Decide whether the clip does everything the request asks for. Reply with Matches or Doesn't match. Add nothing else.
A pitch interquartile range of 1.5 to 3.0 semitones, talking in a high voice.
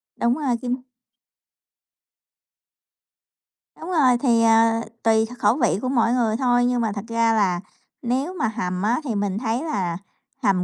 Matches